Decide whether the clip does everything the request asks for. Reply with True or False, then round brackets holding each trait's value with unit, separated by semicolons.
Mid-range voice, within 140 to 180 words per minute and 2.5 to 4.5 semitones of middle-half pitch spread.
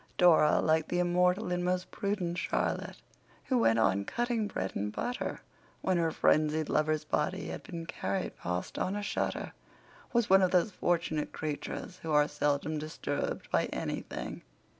True (170 Hz; 160 wpm; 3.5 semitones)